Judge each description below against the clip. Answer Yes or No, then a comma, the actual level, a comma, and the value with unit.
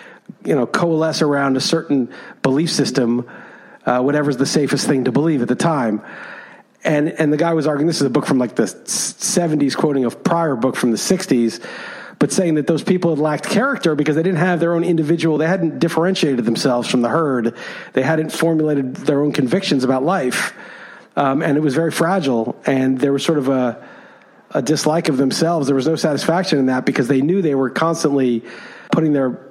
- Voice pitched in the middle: Yes, medium, 150 Hz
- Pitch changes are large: No, average, 3.6 semitones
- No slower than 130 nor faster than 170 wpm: No, average, 200 wpm